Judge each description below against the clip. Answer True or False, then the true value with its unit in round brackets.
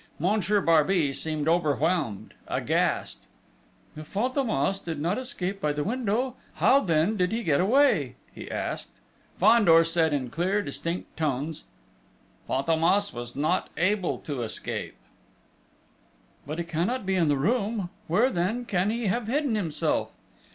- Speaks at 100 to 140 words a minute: True (135 wpm)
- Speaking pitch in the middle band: True (180 Hz)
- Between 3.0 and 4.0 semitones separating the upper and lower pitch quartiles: False (5.5 semitones)